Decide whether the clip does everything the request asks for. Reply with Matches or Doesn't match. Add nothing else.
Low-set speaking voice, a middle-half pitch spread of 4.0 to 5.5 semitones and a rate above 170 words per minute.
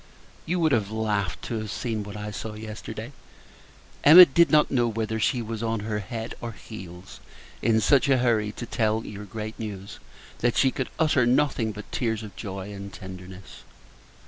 Doesn't match